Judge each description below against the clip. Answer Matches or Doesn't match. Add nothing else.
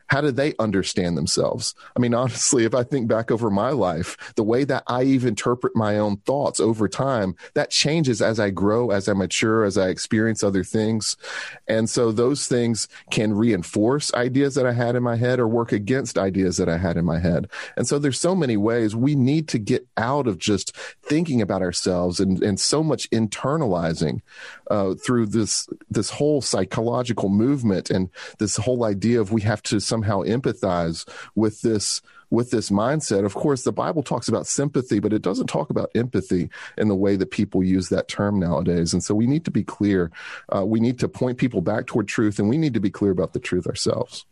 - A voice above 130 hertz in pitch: Doesn't match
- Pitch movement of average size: Matches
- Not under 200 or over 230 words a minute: Matches